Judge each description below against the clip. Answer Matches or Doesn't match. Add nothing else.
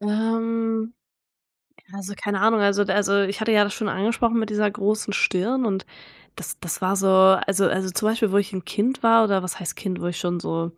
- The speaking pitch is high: Matches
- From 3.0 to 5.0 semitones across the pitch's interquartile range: Doesn't match